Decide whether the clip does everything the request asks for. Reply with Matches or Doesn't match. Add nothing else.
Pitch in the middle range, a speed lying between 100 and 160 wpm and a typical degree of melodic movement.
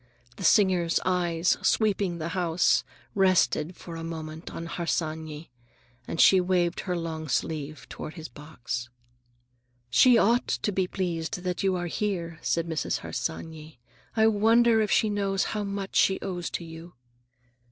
Matches